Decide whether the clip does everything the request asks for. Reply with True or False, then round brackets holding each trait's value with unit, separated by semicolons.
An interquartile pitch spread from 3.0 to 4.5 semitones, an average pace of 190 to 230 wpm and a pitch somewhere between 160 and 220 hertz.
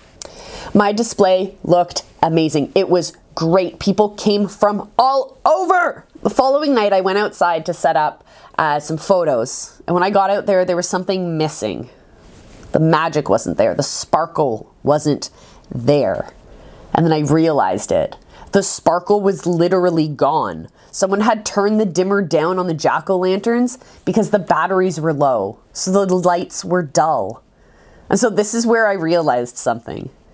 False (4.1 semitones; 160 wpm; 185 Hz)